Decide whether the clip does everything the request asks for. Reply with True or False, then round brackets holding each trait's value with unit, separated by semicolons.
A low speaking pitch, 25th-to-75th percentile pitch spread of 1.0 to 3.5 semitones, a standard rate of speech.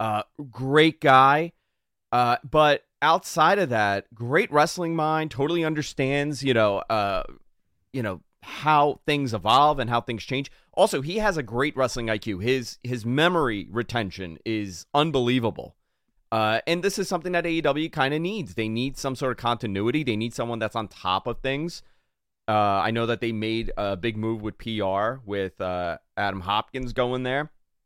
False (125 Hz; 5.1 semitones; 170 wpm)